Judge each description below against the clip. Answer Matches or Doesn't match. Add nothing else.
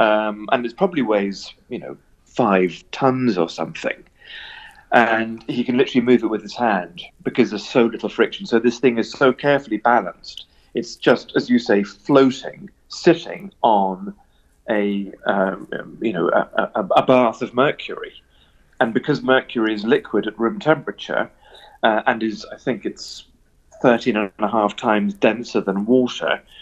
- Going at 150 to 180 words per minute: Matches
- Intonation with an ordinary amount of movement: Matches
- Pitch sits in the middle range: Doesn't match